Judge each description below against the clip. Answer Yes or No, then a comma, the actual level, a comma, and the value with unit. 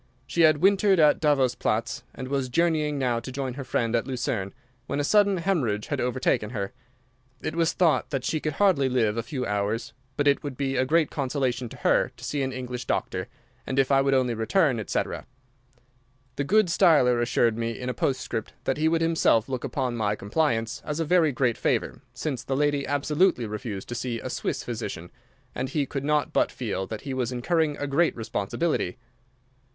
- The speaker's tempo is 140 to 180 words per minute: No, average, 200 wpm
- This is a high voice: No, low, 135 Hz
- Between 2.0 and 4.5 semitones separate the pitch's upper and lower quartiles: Yes, average, 4.1 semitones